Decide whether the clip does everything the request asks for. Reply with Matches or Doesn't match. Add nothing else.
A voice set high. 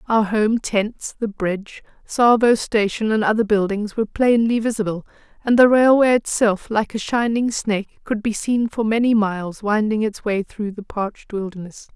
Matches